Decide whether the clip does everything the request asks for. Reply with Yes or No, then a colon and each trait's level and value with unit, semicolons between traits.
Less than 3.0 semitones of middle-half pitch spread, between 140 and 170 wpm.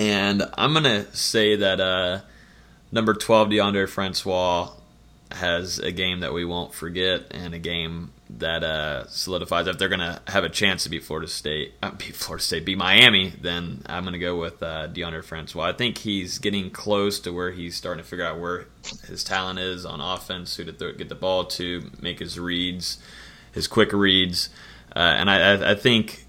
No: narrow, 2.4 semitones; average, 190 wpm